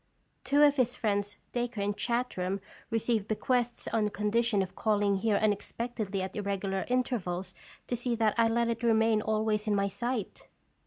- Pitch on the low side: No, high, 220 Hz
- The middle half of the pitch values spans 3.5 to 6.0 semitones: No, average, 2.8 semitones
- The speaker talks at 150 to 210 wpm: Yes, average, 165 wpm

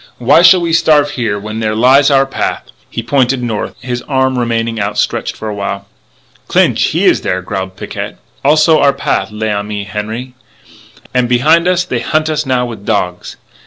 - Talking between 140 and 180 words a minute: Yes, average, 175 wpm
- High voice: No, low, 125 Hz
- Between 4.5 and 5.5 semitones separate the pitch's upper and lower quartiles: Yes, average, 4.9 semitones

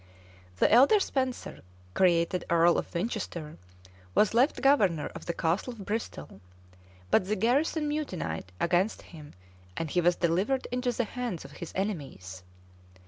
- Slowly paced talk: No, average, 145 wpm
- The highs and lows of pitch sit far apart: Yes, wide, 6.7 semitones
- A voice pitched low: No, medium, 185 Hz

